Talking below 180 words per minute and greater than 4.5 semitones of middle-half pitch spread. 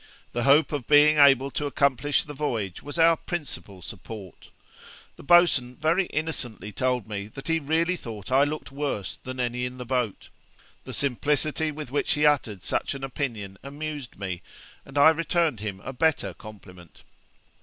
Yes: average, 165 wpm; average, 5.1 semitones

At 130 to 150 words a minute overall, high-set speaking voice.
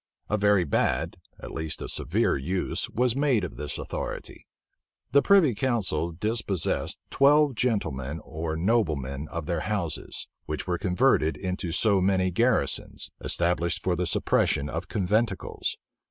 No: average, 140 wpm; very low, 90 Hz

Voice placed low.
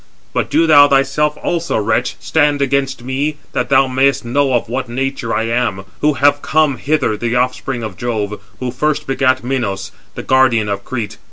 Yes: low, 130 Hz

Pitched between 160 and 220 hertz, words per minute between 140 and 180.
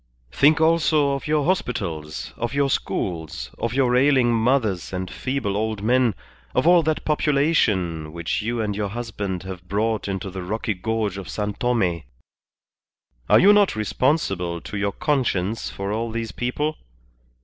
No: low, 110 Hz; average, 155 wpm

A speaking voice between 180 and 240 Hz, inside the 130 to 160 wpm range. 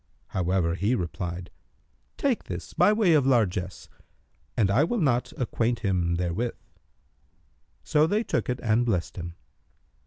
No: low, 110 Hz; slow, 135 wpm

